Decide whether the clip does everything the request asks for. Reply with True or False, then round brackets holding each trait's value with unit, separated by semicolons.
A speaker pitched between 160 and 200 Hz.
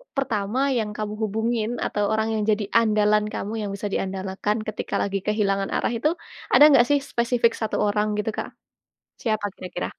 False (215 Hz)